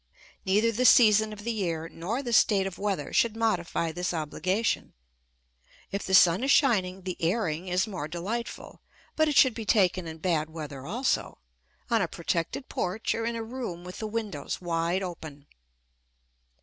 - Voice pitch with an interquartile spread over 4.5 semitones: Yes, average, 5.0 semitones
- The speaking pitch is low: No, high, 190 Hz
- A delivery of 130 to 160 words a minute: No, average, 170 wpm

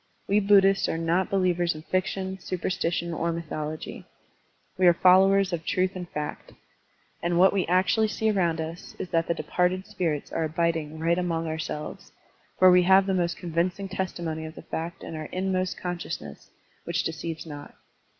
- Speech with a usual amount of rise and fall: No, narrow, 2.3 semitones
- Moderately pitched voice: Yes, medium, 175 Hz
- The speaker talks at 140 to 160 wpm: No, average, 170 wpm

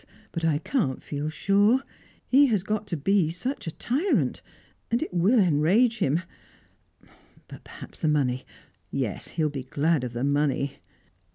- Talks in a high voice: No, medium, 165 Hz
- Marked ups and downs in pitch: Yes, wide, 6.8 semitones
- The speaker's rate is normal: Yes, average, 160 wpm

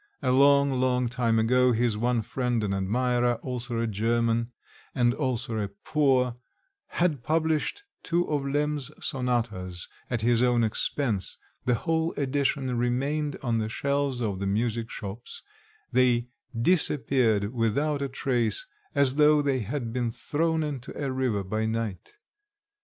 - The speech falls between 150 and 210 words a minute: No, average, 140 wpm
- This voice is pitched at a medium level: No, low, 125 Hz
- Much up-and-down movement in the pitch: No, average, 3.5 semitones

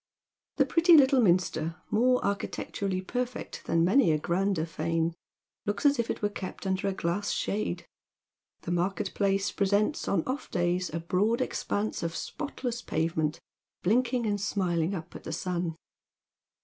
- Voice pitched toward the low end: No, high, 195 Hz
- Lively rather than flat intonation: No, average, 4.6 semitones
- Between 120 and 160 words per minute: Yes, average, 150 wpm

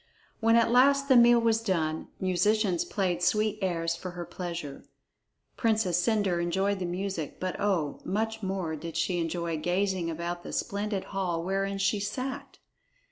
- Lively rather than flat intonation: No, average, 3.6 semitones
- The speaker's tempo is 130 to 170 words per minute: Yes, average, 155 wpm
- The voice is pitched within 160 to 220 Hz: Yes, high, 190 Hz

